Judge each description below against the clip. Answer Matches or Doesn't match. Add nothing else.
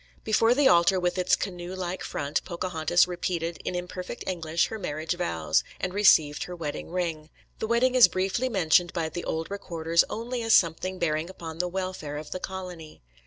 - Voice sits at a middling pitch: Matches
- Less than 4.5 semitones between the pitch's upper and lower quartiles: Matches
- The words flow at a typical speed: Matches